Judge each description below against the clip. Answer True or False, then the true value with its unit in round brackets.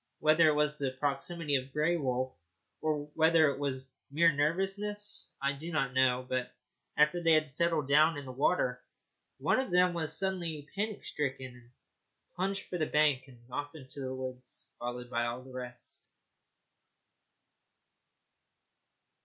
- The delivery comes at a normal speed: True (155 wpm)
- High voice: False (145 Hz)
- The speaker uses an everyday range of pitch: True (4.2 semitones)